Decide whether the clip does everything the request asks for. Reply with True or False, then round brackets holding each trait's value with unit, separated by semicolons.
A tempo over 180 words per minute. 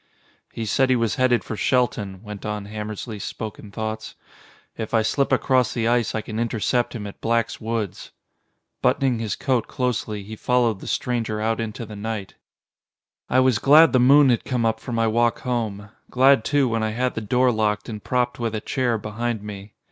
True (195 wpm)